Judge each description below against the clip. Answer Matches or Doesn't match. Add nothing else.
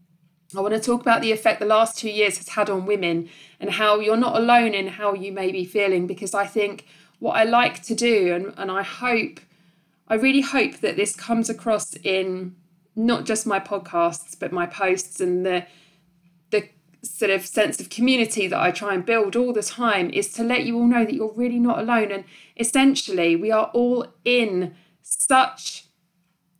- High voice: Matches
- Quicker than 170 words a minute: Matches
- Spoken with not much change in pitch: Doesn't match